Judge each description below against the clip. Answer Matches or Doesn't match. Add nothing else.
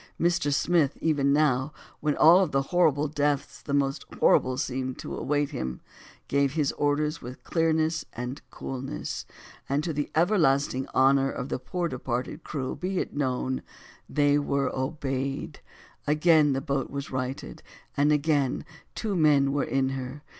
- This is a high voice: Doesn't match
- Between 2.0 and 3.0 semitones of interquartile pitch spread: Matches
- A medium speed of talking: Matches